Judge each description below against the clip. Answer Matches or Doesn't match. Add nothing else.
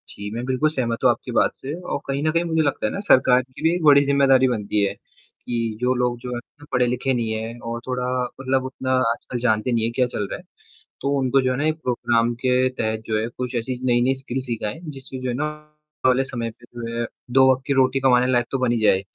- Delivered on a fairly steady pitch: Matches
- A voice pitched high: Doesn't match